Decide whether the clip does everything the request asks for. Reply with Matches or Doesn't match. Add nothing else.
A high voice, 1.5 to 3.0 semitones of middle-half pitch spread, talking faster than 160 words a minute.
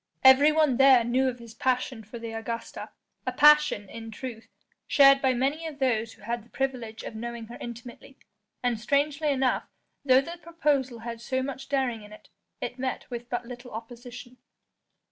Matches